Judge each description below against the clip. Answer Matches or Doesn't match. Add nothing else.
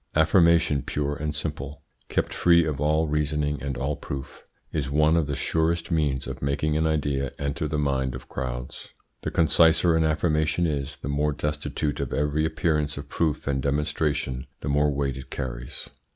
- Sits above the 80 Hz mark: Doesn't match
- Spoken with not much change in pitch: Matches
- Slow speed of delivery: Doesn't match